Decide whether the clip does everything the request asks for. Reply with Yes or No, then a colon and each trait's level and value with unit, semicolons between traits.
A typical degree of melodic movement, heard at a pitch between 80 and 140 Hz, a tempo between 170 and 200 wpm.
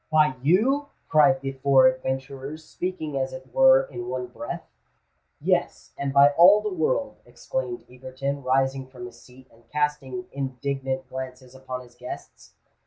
No: average, 3.3 semitones; low, 135 Hz; average, 145 wpm